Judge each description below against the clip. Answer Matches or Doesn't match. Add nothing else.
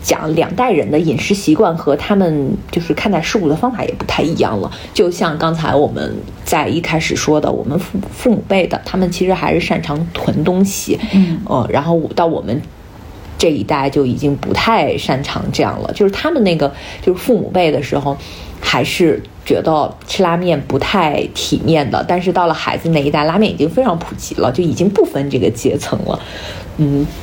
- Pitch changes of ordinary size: Matches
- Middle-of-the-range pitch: Matches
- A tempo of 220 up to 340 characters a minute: Matches